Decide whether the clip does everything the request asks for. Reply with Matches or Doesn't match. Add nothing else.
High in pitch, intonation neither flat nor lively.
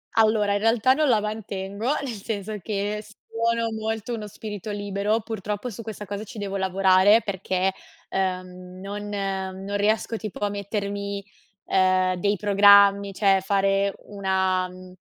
Doesn't match